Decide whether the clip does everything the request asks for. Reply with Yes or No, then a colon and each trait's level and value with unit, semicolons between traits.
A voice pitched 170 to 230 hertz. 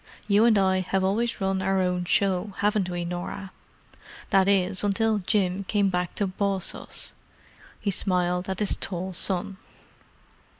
Yes: high, 190 Hz